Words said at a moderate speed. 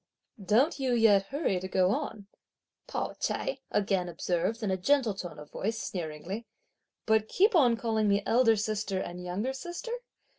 Yes: average, 160 wpm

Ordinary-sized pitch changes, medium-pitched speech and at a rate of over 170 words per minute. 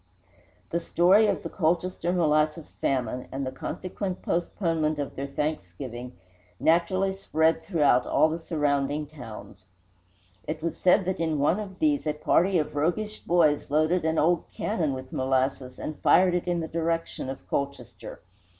No: average, 3.8 semitones; medium, 160 Hz; average, 155 wpm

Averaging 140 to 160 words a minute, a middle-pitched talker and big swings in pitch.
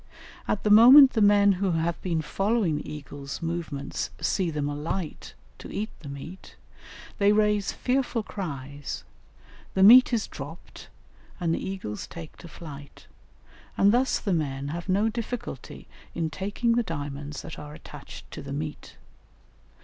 Yes: average, 150 wpm; medium, 175 Hz; wide, 6.0 semitones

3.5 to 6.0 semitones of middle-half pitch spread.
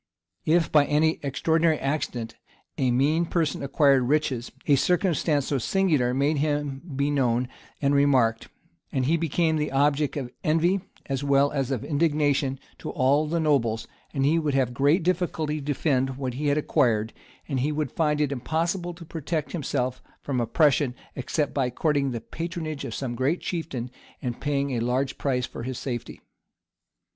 No: average, 3.1 semitones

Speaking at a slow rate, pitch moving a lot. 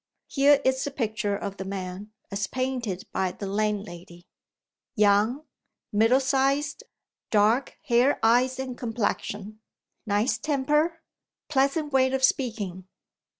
No: slow, 115 wpm; average, 4.6 semitones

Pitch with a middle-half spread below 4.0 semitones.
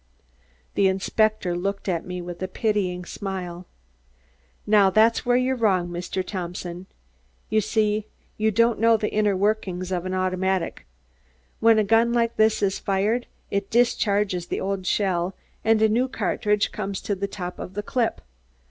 Yes: average, 2.9 semitones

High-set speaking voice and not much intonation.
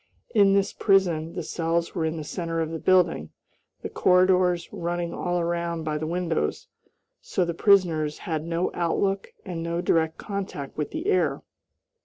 No: medium, 170 Hz; narrow, 2.1 semitones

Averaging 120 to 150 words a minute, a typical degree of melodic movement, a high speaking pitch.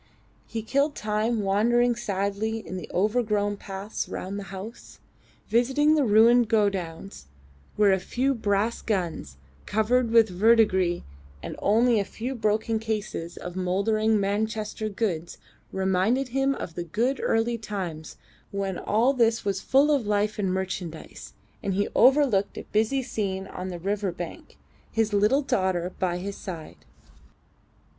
Yes: average, 140 wpm; average, 3.3 semitones; high, 210 Hz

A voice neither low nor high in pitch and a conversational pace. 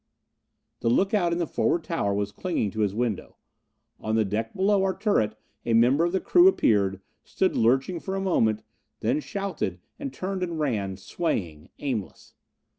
No: low, 130 Hz; average, 175 wpm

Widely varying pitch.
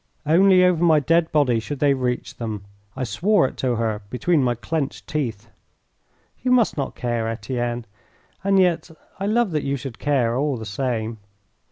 Yes: wide, 5.8 semitones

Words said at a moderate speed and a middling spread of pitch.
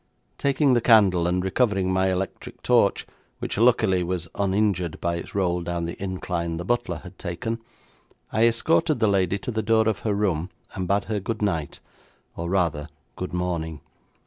Yes: average, 170 wpm; average, 3.9 semitones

